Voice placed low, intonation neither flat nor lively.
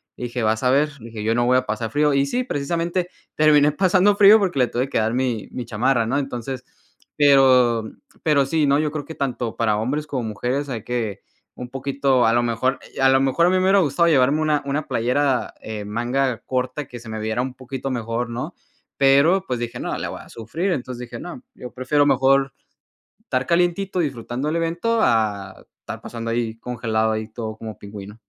Yes: low, 130 Hz; average, 4.1 semitones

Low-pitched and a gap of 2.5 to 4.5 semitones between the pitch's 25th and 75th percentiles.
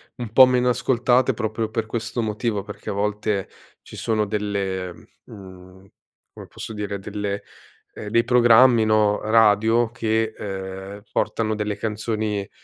No: low, 110 Hz; narrow, 2.1 semitones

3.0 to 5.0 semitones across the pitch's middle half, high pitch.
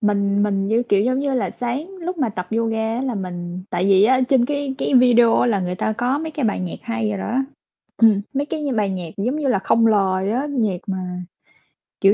Yes: average, 4.5 semitones; high, 225 Hz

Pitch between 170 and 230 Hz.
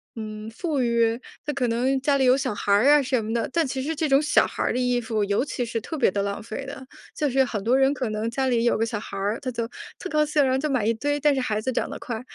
No: very high, 250 Hz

